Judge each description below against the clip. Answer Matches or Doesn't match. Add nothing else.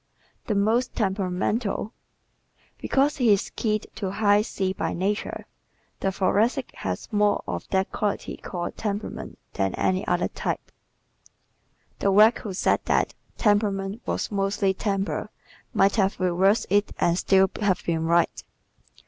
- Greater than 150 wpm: Doesn't match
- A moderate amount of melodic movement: Doesn't match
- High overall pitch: Matches